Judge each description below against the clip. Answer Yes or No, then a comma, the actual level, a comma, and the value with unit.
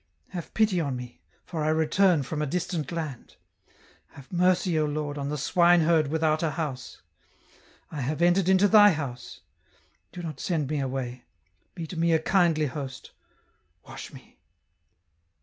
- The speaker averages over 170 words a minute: No, average, 160 wpm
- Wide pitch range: No, average, 3.4 semitones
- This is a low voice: No, medium, 155 Hz